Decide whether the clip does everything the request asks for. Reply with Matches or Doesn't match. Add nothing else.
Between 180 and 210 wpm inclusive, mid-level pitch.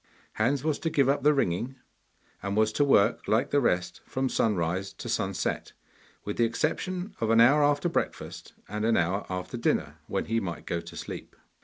Doesn't match